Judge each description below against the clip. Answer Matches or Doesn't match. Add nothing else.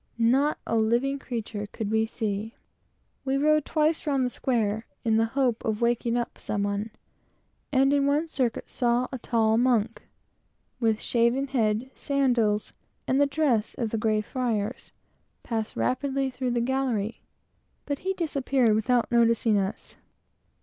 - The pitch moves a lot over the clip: Doesn't match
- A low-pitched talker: Doesn't match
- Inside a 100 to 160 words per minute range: Matches